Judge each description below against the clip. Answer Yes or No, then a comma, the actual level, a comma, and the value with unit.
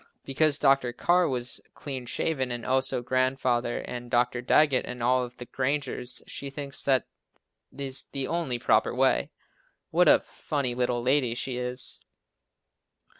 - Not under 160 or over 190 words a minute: No, average, 145 wpm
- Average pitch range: No, narrow, 2.0 semitones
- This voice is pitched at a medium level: No, low, 130 Hz